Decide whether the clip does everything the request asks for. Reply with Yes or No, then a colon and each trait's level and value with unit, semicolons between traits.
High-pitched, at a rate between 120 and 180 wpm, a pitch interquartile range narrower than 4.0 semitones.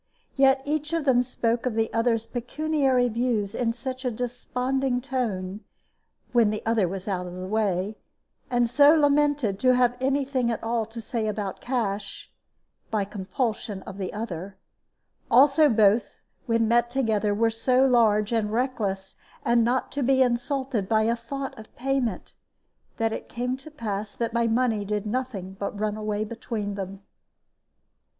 Yes: high, 230 Hz; average, 160 wpm; average, 3.5 semitones